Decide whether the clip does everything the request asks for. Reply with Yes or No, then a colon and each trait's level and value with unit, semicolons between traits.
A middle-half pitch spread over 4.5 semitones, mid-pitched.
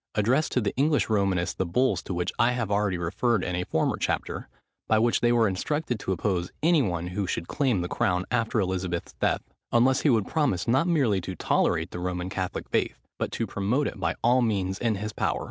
No: average, 5.0 semitones; low, 105 Hz